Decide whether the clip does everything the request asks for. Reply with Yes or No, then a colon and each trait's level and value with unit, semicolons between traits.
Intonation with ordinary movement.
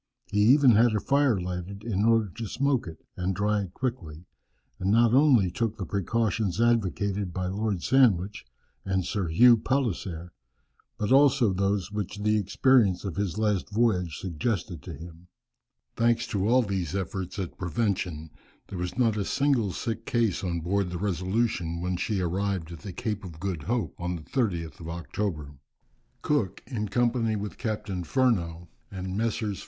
Yes: average, 4.3 semitones